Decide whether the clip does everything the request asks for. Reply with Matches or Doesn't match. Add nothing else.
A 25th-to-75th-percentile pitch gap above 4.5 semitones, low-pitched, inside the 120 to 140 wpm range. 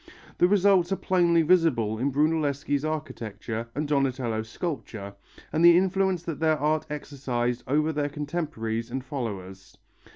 Doesn't match